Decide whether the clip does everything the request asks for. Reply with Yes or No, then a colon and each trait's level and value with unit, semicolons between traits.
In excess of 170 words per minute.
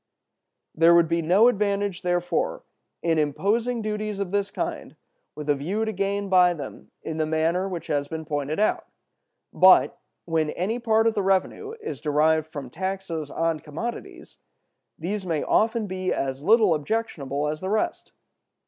No: average, 160 wpm